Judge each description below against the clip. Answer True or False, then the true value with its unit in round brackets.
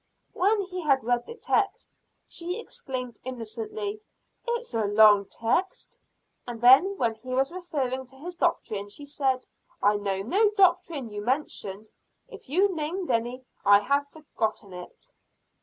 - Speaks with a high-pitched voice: True (265 Hz)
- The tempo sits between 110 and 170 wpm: True (145 wpm)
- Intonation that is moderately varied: False (8.1 semitones)